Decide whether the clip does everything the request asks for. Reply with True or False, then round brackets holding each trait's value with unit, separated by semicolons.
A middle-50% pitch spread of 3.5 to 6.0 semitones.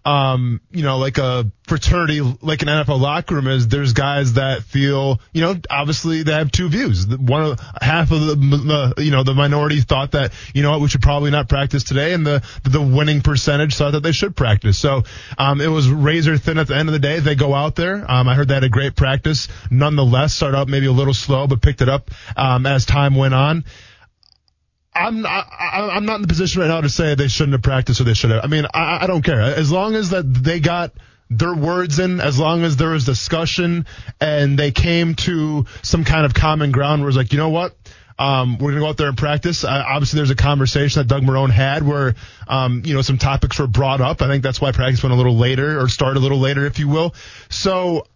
False (2.8 semitones)